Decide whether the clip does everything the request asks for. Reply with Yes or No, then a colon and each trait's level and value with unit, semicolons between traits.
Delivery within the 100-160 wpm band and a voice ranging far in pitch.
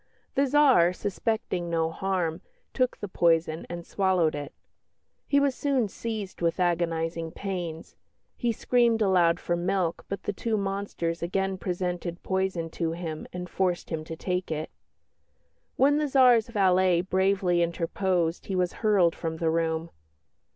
No: average, 145 wpm; average, 3.0 semitones